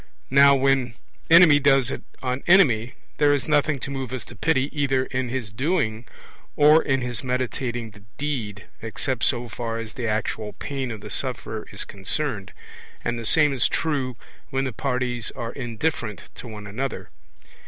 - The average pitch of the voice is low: Yes, low, 130 Hz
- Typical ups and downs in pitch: Yes, average, 3.4 semitones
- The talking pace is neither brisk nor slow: Yes, average, 170 wpm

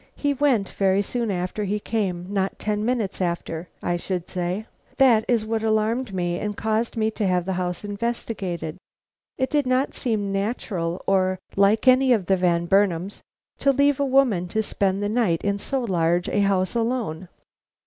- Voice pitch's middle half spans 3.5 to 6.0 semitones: Yes, average, 4.0 semitones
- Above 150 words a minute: Yes, average, 180 wpm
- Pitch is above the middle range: Yes, high, 205 Hz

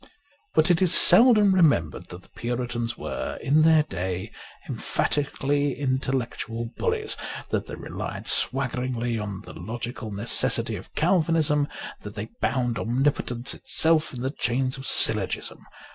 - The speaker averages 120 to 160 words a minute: Yes, slow, 135 wpm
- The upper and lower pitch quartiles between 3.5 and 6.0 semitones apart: Yes, average, 4.5 semitones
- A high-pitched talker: No, low, 130 Hz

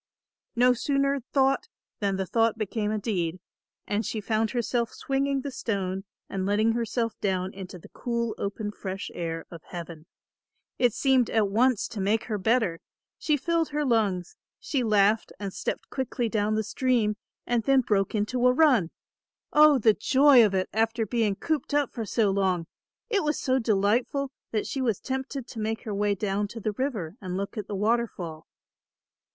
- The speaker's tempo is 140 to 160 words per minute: No, average, 180 wpm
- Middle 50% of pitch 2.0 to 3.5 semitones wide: No, average, 4.2 semitones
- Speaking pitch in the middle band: No, high, 220 Hz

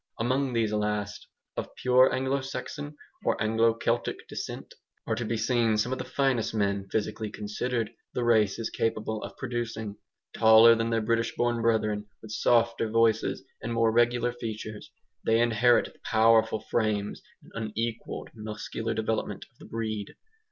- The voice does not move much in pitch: Yes, narrow, 1.6 semitones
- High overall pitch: No, low, 115 Hz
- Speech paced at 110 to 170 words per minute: Yes, average, 155 wpm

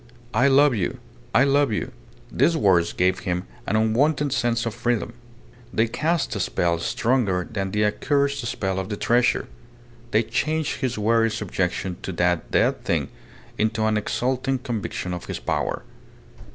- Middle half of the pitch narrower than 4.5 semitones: No, average, 5.2 semitones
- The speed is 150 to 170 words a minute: Yes, average, 155 wpm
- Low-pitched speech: Yes, low, 115 Hz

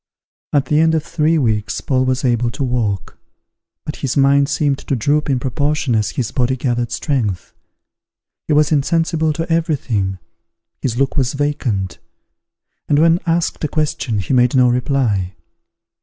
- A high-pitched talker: No, low, 135 Hz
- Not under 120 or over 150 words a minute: No, average, 160 wpm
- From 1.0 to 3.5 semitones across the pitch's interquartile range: No, average, 3.9 semitones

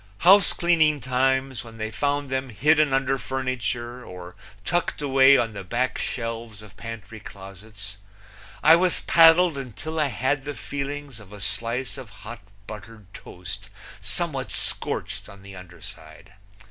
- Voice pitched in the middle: No, low, 120 Hz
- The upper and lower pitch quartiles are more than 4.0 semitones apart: Yes, wide, 5.4 semitones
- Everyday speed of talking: Yes, average, 145 wpm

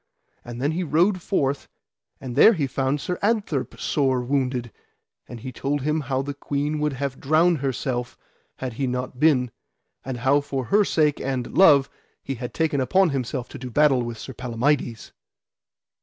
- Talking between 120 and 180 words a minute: Yes, average, 170 wpm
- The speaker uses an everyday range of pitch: Yes, average, 3.0 semitones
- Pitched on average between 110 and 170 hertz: Yes, low, 135 Hz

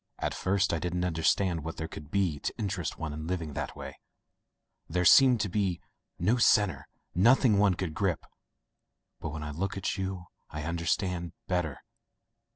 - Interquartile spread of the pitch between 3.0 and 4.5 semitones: Yes, average, 3.3 semitones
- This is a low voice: Yes, very low, 90 Hz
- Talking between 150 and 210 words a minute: Yes, average, 170 wpm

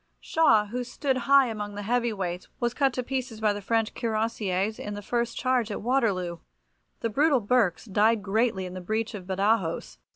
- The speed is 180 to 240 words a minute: Yes, average, 190 wpm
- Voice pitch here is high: Yes, high, 220 Hz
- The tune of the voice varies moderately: Yes, average, 3.5 semitones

